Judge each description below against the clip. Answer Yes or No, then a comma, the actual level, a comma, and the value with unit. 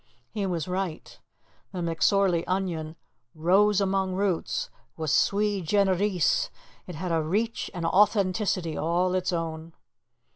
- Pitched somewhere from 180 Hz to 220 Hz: Yes, medium, 185 Hz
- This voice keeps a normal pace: No, slow, 120 wpm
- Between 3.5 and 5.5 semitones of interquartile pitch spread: No, average, 3.1 semitones